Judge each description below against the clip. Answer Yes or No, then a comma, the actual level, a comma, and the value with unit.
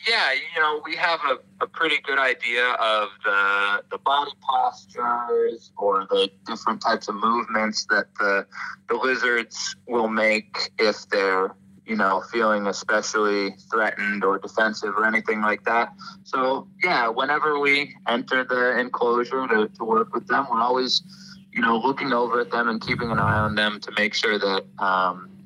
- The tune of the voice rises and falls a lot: Yes, wide, 6.2 semitones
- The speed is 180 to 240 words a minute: No, average, 165 wpm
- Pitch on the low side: Yes, low, 120 Hz